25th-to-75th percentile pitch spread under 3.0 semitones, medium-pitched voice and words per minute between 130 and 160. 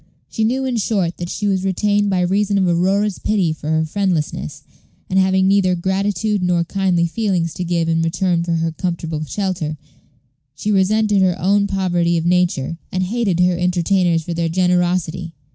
No: narrow, 2.6 semitones; medium, 180 Hz; average, 175 wpm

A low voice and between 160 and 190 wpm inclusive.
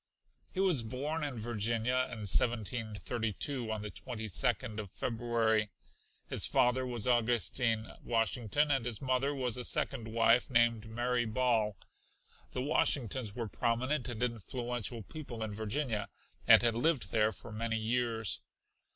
No: low, 120 Hz; slow, 135 wpm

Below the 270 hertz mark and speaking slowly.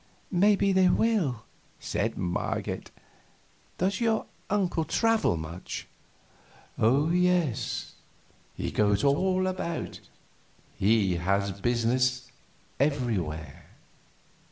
Yes: low, 135 Hz; slow, 85 wpm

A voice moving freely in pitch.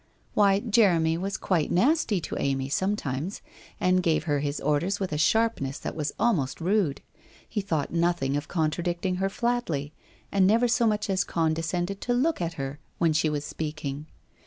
No: average, 4.8 semitones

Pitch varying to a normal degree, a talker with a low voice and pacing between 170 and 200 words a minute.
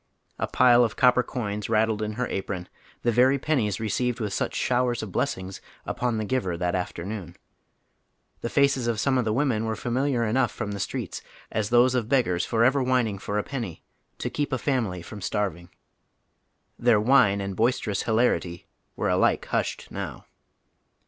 Yes: average, 3.6 semitones; low, 115 Hz; average, 175 wpm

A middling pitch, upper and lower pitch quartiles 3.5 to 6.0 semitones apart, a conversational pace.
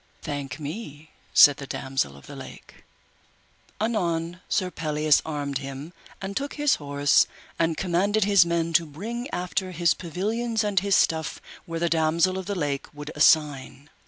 Yes: medium, 165 Hz; average, 4.6 semitones; average, 160 wpm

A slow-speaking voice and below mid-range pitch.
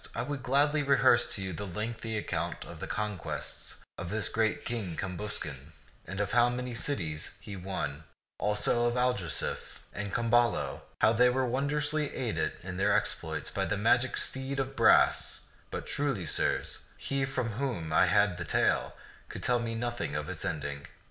No: average, 170 wpm; low, 110 Hz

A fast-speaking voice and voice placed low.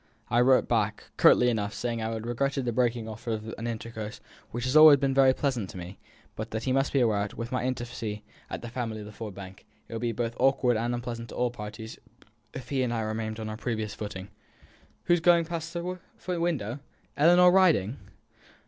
Yes: fast, 215 wpm; low, 120 Hz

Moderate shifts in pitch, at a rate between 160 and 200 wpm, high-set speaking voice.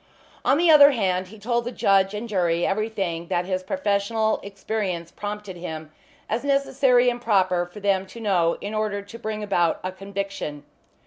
Yes: average, 3.3 semitones; average, 175 wpm; high, 200 Hz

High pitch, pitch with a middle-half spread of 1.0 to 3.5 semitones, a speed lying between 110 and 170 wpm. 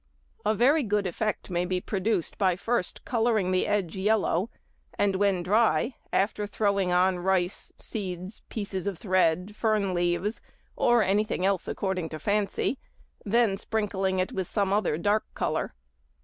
Yes: high, 195 Hz; narrow, 2.6 semitones; average, 145 wpm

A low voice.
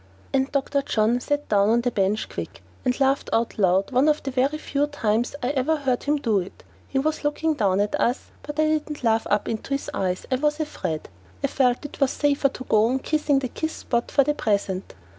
No: very high, 260 Hz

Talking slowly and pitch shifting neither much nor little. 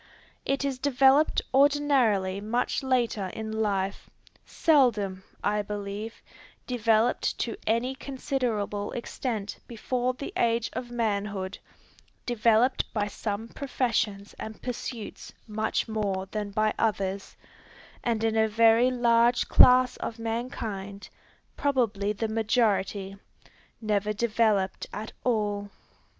Yes: slow, 110 wpm; average, 3.1 semitones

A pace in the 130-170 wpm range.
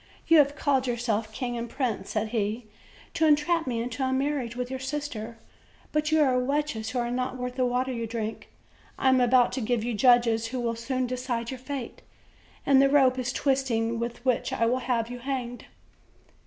No: fast, 205 wpm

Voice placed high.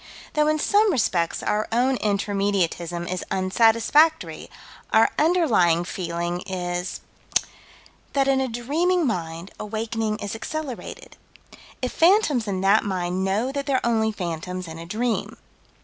Yes: high, 215 Hz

